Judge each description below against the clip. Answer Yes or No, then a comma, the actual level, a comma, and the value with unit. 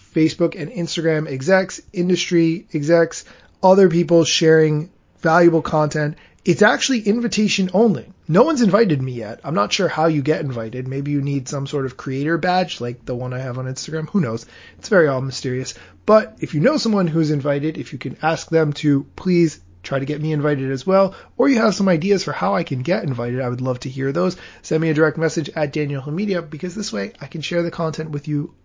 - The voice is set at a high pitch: No, medium, 160 Hz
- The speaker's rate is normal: No, fast, 215 wpm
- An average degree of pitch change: Yes, average, 4.4 semitones